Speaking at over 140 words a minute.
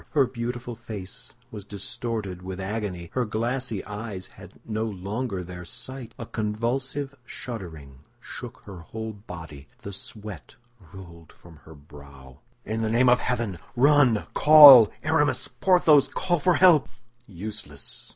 No: slow, 135 wpm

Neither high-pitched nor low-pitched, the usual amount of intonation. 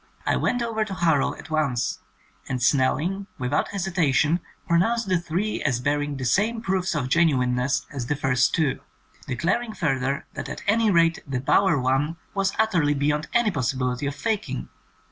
No: medium, 150 Hz; wide, 6.4 semitones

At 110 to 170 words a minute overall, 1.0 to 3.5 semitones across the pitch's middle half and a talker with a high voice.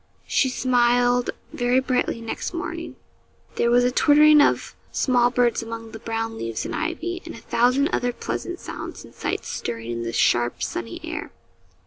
Yes: average, 165 wpm; average, 2.7 semitones; high, 245 Hz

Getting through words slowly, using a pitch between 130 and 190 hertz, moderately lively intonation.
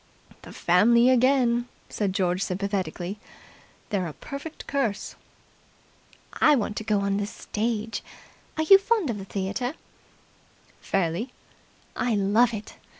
No: slow, 125 wpm; high, 215 Hz; average, 4.0 semitones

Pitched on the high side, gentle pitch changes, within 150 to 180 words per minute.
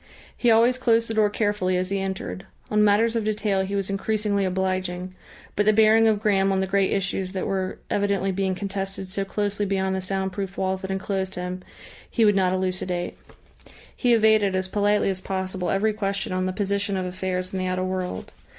No: high, 195 Hz; narrow, 1.7 semitones; average, 200 wpm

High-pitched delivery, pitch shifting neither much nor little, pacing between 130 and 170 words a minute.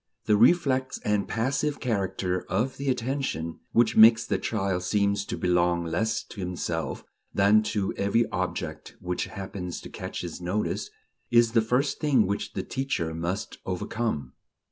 No: low, 105 Hz; average, 4.6 semitones; average, 150 wpm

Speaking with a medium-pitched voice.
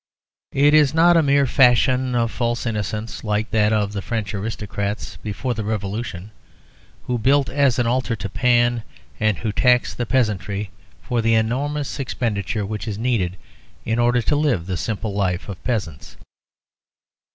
No: low, 115 Hz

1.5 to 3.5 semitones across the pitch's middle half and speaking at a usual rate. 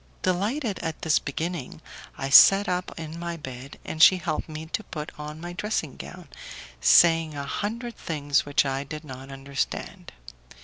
No: average, 4.0 semitones; average, 165 wpm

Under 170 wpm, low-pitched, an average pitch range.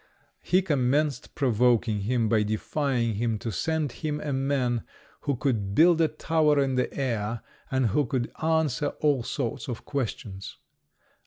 Yes: average, 150 wpm; low, 130 Hz; average, 4.4 semitones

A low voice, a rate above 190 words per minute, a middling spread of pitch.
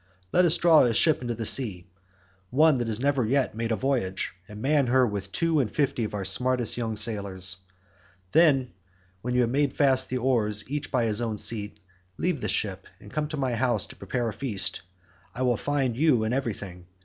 Yes: low, 120 Hz; average, 200 wpm; average, 4.5 semitones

